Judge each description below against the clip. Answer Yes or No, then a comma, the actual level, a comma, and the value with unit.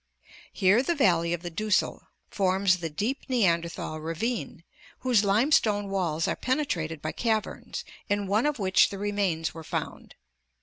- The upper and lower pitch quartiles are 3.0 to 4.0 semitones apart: No, average, 4.6 semitones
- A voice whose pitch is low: No, high, 195 Hz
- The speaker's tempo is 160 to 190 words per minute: No, average, 145 wpm